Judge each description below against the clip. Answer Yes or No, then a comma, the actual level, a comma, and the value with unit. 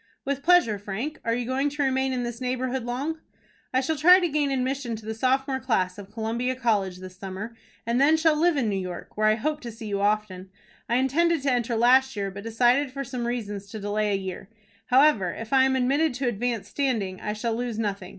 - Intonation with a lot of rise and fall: No, average, 4.0 semitones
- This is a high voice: Yes, high, 240 Hz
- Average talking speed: No, fast, 225 wpm